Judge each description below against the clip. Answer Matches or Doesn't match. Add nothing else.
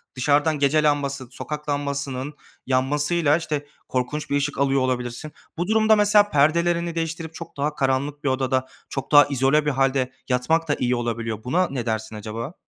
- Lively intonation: Doesn't match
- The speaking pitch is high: Doesn't match